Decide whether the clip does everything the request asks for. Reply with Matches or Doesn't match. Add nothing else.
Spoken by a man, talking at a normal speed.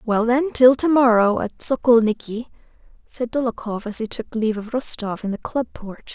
Doesn't match